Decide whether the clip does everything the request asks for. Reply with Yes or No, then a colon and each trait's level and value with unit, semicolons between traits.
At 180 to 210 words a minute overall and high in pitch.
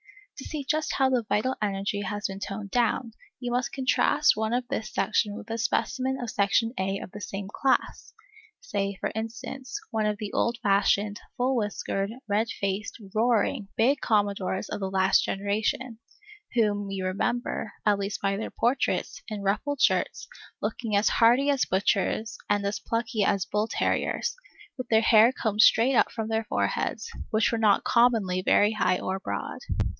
No: average, 170 wpm; high, 215 Hz